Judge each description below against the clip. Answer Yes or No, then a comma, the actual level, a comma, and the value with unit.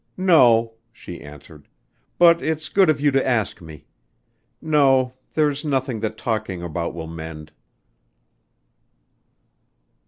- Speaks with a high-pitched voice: No, low, 120 Hz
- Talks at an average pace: No, slow, 115 wpm